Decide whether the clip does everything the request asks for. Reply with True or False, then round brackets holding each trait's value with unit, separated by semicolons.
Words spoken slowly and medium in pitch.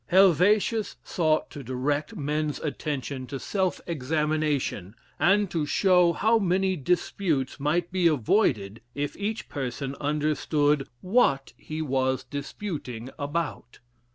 True (115 wpm; 150 Hz)